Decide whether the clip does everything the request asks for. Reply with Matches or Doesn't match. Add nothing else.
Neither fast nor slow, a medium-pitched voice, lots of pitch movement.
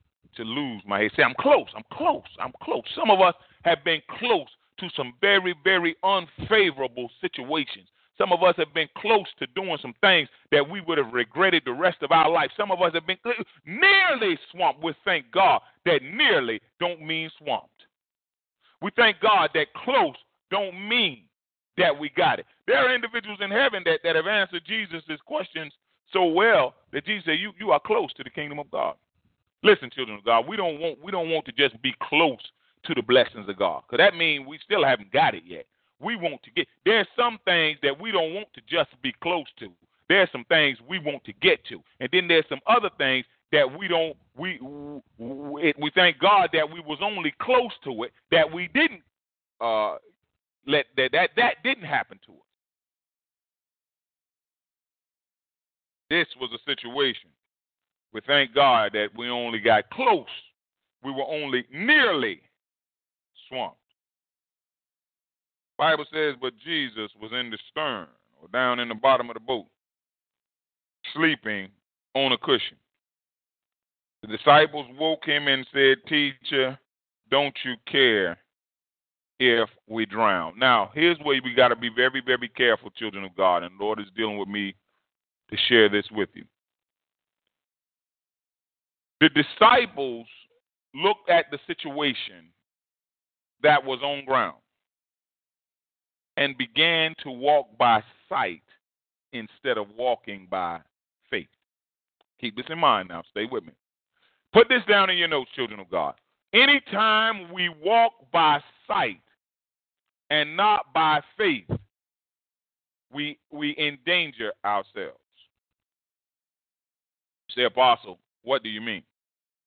Matches